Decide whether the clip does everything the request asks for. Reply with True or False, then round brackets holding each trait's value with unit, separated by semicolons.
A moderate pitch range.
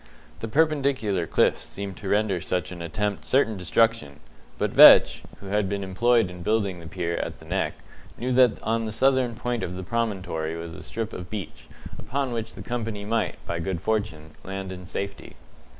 True (4.1 semitones)